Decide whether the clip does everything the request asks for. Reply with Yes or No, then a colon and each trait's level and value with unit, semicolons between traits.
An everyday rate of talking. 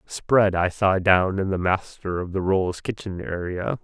Yes: average, 190 wpm